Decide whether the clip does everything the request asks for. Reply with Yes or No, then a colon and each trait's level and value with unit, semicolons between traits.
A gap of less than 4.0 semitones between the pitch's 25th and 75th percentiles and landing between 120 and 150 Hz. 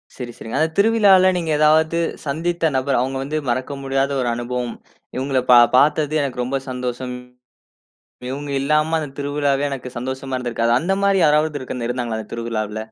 Yes: average, 3.6 semitones; low, 135 Hz